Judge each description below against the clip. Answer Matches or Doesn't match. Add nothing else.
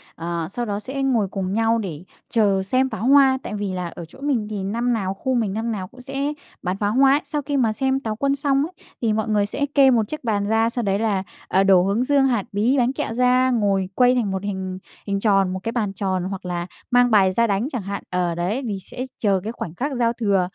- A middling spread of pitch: Matches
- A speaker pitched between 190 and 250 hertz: Matches